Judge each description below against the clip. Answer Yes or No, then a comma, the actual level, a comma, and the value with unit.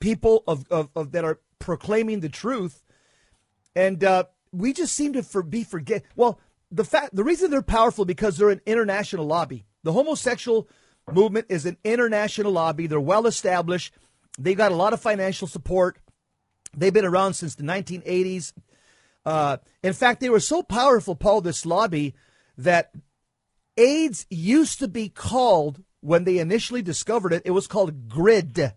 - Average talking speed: Yes, average, 165 wpm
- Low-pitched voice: No, medium, 185 Hz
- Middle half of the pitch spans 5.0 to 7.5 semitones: Yes, average, 5.3 semitones